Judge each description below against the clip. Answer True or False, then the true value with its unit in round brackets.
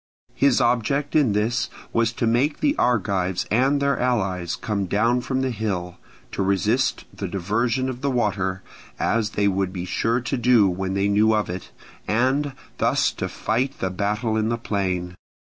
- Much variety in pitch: False (4.3 semitones)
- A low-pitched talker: True (110 Hz)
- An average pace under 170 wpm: False (175 wpm)